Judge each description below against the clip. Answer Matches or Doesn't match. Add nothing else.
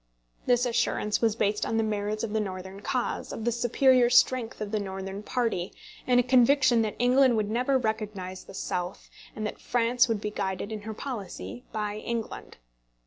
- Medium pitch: Doesn't match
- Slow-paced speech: Doesn't match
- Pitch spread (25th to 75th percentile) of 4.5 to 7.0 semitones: Doesn't match